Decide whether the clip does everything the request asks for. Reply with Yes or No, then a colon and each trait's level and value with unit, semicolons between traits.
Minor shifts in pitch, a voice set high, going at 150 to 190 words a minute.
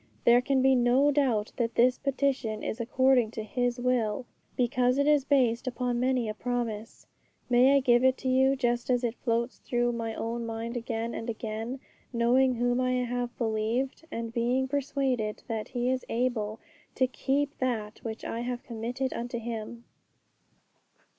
Yes: narrow, 2.0 semitones; high, 245 Hz; average, 165 wpm